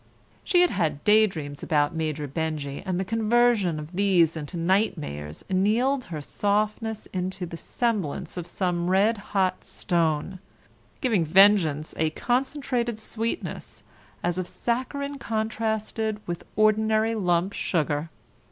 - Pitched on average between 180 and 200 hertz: Yes, high, 190 Hz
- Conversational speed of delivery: No, slow, 125 wpm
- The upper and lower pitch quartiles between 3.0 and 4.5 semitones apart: No, average, 5.2 semitones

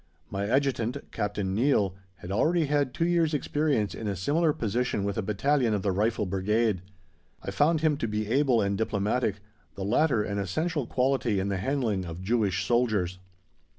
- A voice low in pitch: Yes, low, 110 Hz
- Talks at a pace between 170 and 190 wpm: Yes, average, 175 wpm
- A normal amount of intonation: No, wide, 5.7 semitones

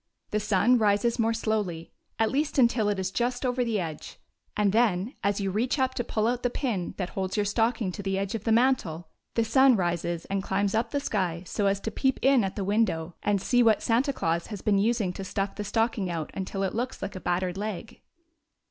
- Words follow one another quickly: Yes, fast, 230 wpm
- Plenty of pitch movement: No, average, 3.6 semitones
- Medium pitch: No, high, 210 Hz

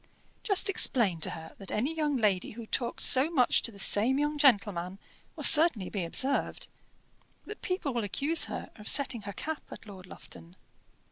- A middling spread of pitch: No, wide, 6.7 semitones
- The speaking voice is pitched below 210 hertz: No, high, 235 Hz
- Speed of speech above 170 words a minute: Yes, average, 180 wpm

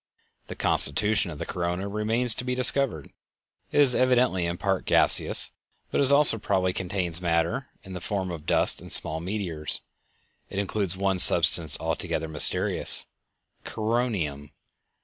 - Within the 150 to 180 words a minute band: No, average, 140 wpm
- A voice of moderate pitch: No, very low, 95 Hz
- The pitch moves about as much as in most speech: Yes, average, 4.6 semitones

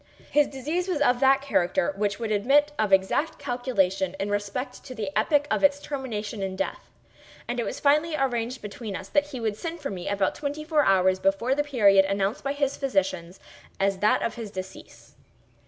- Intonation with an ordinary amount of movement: No, wide, 6.3 semitones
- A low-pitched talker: No, high, 230 Hz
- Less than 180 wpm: No, average, 195 wpm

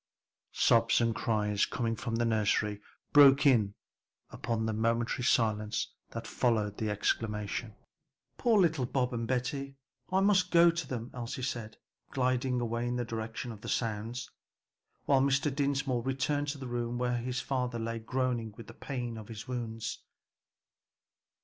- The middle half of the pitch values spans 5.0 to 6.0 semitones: No, average, 2.7 semitones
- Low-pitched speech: Yes, low, 120 Hz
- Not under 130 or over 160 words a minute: Yes, average, 155 wpm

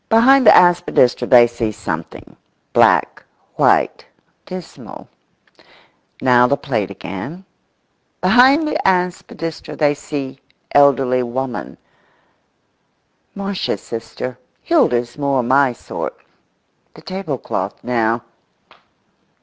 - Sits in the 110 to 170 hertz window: Yes, low, 135 Hz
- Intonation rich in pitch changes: Yes, wide, 6.9 semitones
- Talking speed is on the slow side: Yes, slow, 90 wpm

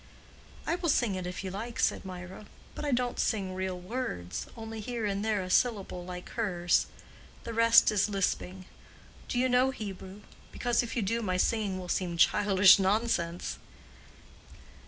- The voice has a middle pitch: No, high, 200 Hz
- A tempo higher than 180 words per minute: No, average, 155 wpm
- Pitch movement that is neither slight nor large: Yes, average, 3.8 semitones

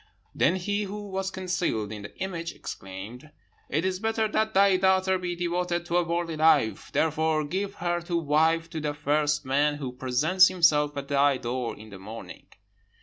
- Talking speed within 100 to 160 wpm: No, average, 180 wpm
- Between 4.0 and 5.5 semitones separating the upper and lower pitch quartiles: Yes, average, 4.5 semitones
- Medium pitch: Yes, medium, 165 Hz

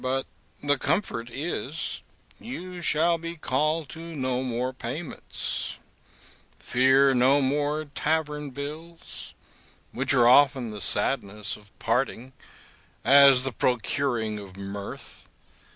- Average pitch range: Yes, average, 4.0 semitones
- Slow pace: Yes, slow, 110 wpm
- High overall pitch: No, low, 135 Hz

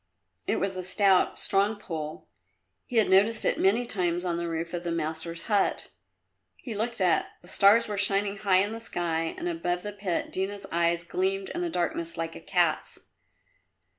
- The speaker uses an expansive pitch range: No, average, 3.2 semitones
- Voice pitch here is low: No, medium, 185 Hz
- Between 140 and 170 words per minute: No, average, 185 wpm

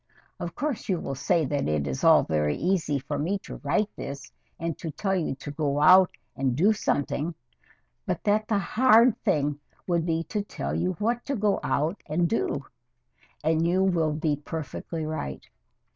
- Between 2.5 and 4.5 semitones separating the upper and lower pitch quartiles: No, average, 4.9 semitones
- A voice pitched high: No, medium, 165 Hz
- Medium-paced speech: Yes, average, 180 wpm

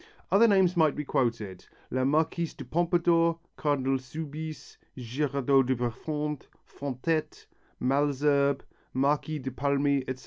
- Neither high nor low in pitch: Yes, medium, 145 Hz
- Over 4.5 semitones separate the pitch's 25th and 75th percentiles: No, average, 3.0 semitones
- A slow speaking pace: Yes, slow, 115 wpm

